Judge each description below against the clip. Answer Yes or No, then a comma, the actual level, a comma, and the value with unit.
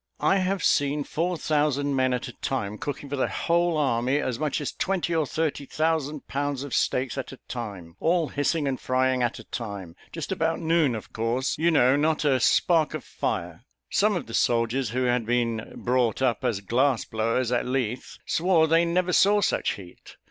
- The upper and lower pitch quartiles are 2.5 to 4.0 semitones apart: No, average, 4.7 semitones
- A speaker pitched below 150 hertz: Yes, low, 135 Hz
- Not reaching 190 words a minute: No, average, 195 wpm